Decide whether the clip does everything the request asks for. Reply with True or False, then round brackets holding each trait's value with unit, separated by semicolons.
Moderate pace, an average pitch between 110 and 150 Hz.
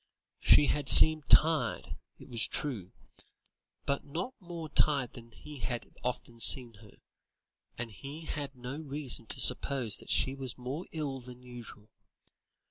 True (145 wpm; 135 Hz)